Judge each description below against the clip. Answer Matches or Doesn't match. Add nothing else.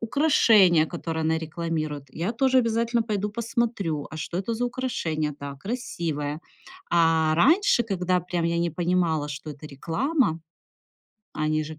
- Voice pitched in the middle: Matches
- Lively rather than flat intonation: Matches